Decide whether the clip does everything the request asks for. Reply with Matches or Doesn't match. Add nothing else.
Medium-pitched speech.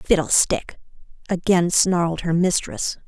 Matches